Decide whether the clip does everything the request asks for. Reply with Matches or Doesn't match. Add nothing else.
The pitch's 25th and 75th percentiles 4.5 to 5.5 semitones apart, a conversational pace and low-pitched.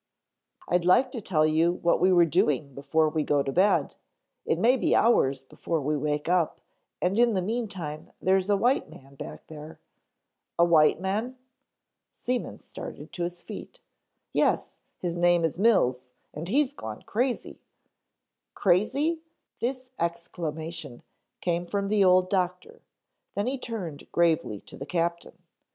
Doesn't match